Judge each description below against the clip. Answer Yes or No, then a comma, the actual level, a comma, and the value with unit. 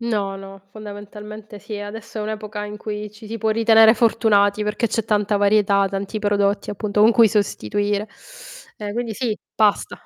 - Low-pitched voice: No, high, 210 Hz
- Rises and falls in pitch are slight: Yes, narrow, 1.2 semitones